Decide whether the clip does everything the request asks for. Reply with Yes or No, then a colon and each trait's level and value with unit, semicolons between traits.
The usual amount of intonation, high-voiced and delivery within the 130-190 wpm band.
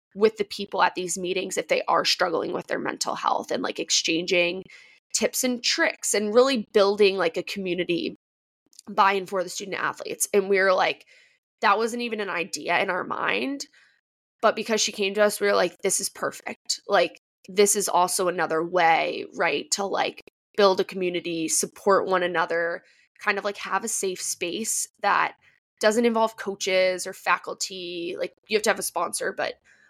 Yes: average, 3.2 semitones; high, 195 Hz; average, 185 wpm